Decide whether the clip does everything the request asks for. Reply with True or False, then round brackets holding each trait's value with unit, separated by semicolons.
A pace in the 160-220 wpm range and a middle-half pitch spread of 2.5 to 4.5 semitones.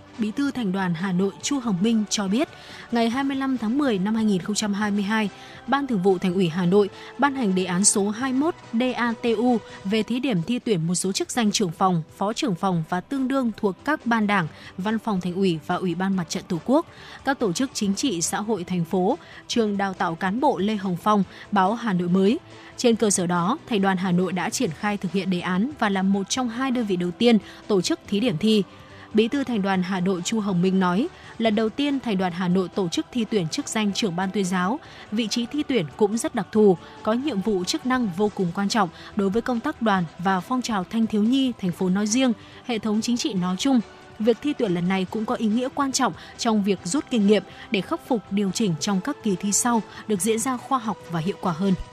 False (245 wpm; 4.0 semitones)